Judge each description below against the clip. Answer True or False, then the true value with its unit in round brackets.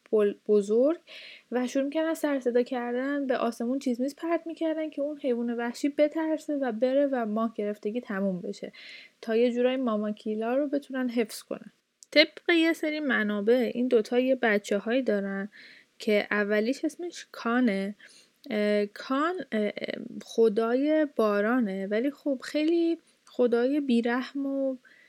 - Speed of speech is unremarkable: True (140 wpm)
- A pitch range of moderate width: True (4.3 semitones)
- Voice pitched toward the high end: True (250 Hz)